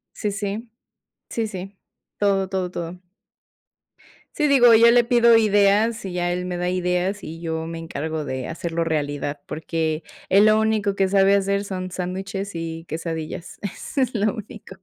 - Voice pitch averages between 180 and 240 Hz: Yes, high, 190 Hz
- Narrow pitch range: No, average, 3.9 semitones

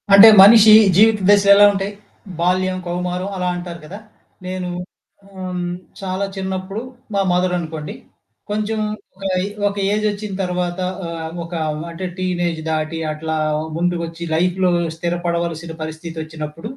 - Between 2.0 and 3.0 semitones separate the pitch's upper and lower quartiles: Yes, narrow, 2.5 semitones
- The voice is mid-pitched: Yes, medium, 180 Hz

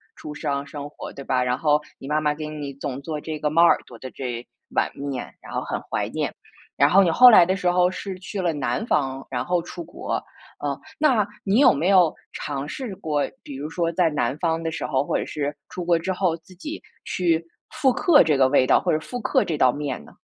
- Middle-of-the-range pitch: Yes, medium, 155 Hz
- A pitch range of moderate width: Yes, average, 4.1 semitones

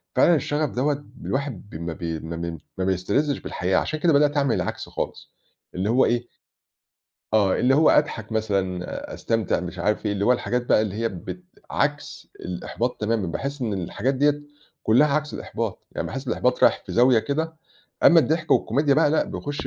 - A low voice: Yes, low, 120 Hz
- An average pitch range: No, wide, 6.7 semitones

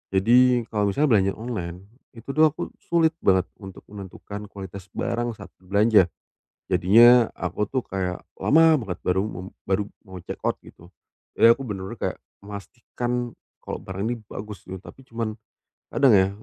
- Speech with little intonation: No, average, 4.0 semitones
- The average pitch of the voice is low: Yes, low, 105 Hz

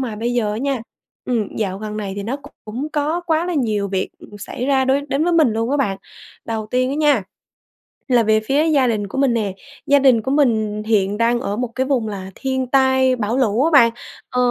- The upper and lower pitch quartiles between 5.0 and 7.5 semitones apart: No, average, 4.2 semitones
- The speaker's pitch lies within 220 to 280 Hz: Yes, high, 245 Hz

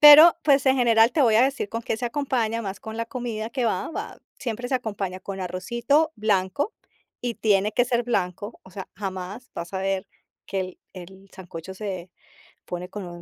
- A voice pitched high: Yes, high, 215 Hz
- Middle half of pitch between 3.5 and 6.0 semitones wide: Yes, average, 4.4 semitones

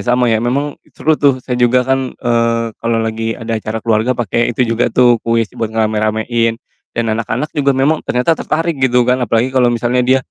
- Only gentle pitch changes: Yes, narrow, 2.3 semitones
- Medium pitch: No, low, 120 Hz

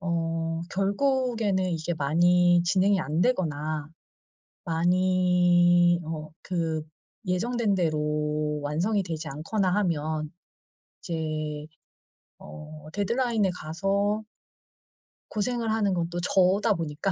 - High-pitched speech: No, medium, 175 Hz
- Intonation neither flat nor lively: Yes, average, 3.9 semitones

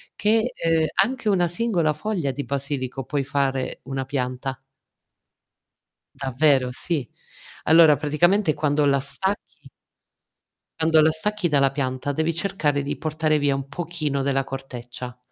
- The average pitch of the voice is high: No, medium, 145 Hz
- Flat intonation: No, average, 3.4 semitones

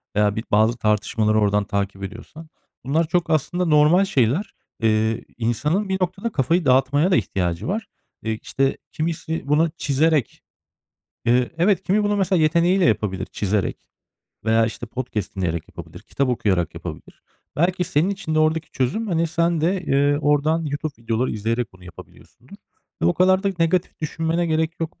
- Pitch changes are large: Yes, wide, 7.2 semitones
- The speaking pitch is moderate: Yes, medium, 145 Hz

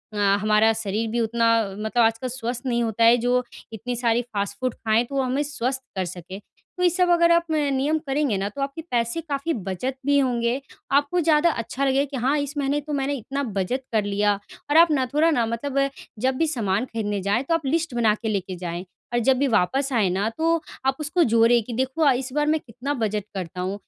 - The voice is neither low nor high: No, high, 245 Hz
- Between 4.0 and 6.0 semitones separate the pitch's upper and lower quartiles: Yes, average, 4.5 semitones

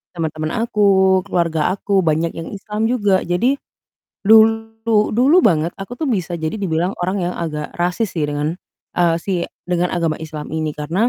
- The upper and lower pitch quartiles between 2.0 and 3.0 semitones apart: No, average, 4.6 semitones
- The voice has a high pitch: No, medium, 180 Hz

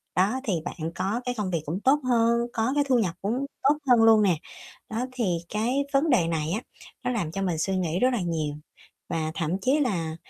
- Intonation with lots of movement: Yes, wide, 6.5 semitones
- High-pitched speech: Yes, high, 215 Hz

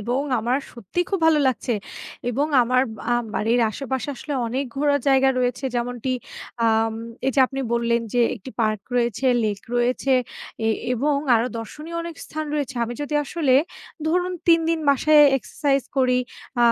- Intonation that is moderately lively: Yes, average, 3.6 semitones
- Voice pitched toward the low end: No, very high, 260 Hz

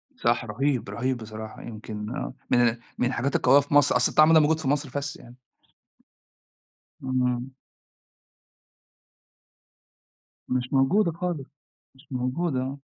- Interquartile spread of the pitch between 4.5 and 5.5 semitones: No, average, 2.8 semitones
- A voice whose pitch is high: No, low, 130 Hz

